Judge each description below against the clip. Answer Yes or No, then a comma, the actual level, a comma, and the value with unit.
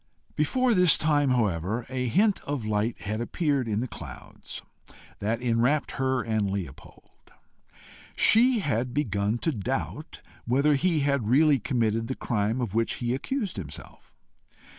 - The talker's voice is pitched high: No, low, 125 Hz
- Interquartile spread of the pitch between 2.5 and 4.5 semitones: No, average, 5.1 semitones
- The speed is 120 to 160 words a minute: Yes, average, 140 wpm